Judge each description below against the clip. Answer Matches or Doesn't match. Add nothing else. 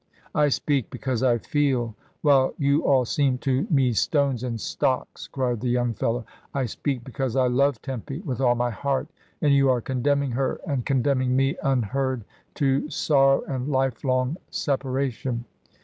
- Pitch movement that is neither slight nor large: Doesn't match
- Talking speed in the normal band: Matches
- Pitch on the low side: Matches